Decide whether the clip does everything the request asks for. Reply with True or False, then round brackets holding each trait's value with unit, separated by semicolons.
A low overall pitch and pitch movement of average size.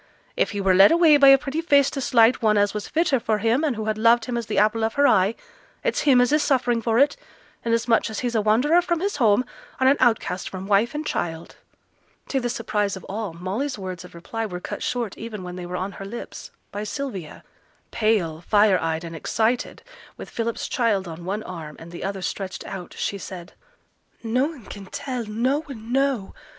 False (220 Hz; 4.8 semitones)